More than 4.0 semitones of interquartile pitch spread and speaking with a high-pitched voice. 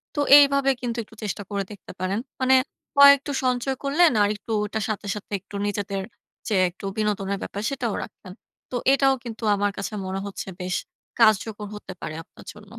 Yes: average, 4.5 semitones; high, 210 Hz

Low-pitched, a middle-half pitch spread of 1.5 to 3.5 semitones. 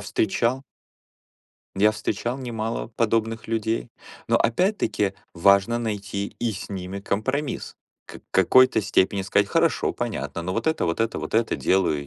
Yes: low, 110 Hz; average, 2.9 semitones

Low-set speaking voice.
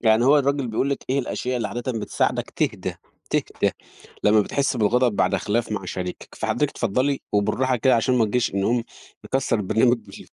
Yes: low, 120 Hz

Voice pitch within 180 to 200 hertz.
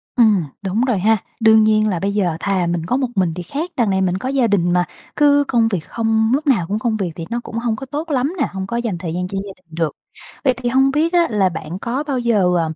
No: high, 215 Hz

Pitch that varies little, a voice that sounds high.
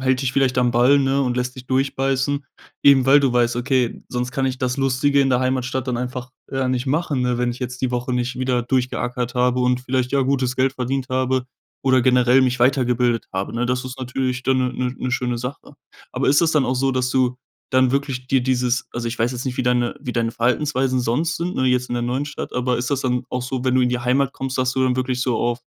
No: narrow, 1.2 semitones; low, 125 Hz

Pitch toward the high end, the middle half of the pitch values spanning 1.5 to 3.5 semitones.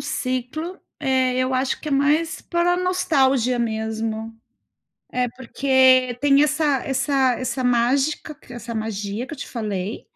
Yes: very high, 260 Hz; average, 3.1 semitones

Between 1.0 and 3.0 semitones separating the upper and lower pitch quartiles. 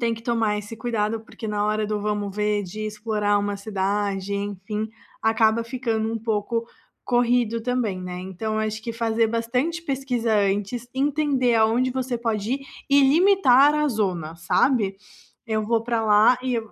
Yes: average, 2.7 semitones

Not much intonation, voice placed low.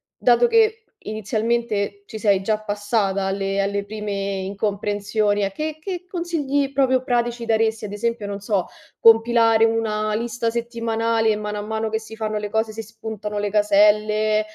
No: narrow, 2.1 semitones; high, 220 Hz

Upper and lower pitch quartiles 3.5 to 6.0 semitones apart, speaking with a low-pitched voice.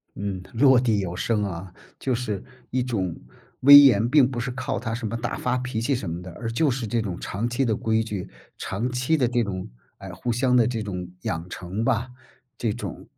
Yes: average, 3.9 semitones; low, 115 Hz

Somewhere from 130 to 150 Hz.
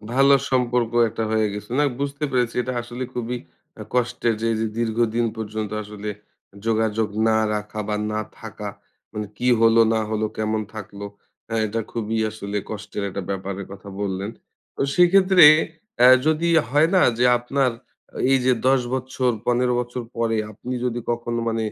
No: low, 115 Hz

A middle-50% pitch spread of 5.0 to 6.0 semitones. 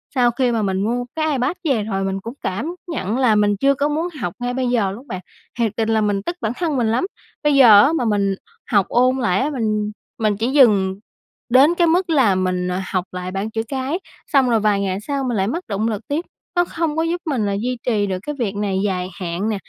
Yes: average, 5.3 semitones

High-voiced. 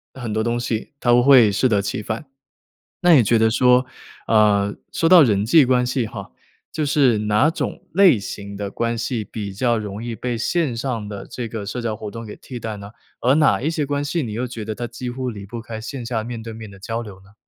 No: low, 115 Hz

